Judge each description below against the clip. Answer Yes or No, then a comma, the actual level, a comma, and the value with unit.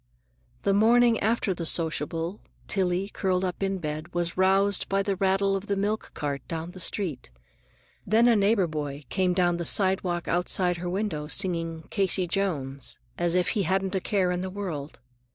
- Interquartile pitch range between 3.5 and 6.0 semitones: No, average, 2.7 semitones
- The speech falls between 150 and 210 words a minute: Yes, average, 175 wpm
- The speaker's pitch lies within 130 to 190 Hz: Yes, medium, 185 Hz